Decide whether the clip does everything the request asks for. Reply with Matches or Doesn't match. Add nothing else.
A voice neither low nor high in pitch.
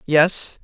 Matches